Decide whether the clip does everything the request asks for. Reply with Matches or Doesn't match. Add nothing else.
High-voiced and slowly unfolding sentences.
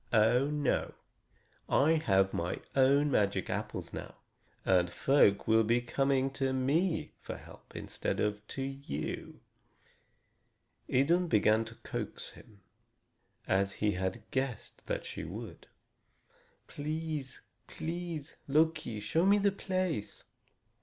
Doesn't match